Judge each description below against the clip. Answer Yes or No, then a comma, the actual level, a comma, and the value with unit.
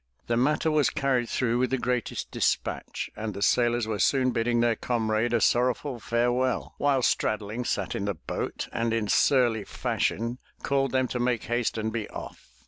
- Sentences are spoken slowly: No, average, 180 wpm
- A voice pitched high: No, low, 120 Hz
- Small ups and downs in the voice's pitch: Yes, narrow, 2.2 semitones